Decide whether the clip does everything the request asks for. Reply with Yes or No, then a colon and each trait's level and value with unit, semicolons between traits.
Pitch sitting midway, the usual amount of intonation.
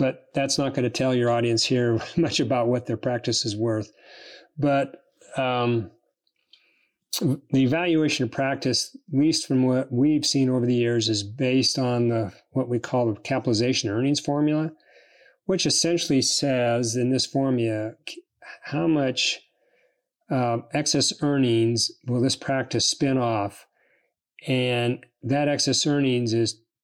No: low, 130 Hz; average, 3.1 semitones